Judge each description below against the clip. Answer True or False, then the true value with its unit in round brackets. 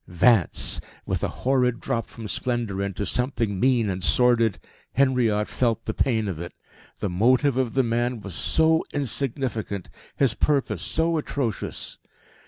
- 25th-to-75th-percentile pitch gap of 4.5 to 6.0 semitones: False (4.0 semitones)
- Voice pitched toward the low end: True (120 Hz)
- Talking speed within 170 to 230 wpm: False (145 wpm)